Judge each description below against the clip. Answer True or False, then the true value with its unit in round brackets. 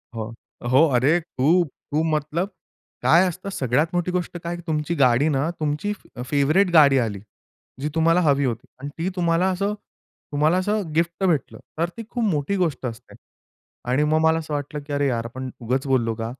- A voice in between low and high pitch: True (150 Hz)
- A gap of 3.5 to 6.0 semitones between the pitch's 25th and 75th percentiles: True (4.4 semitones)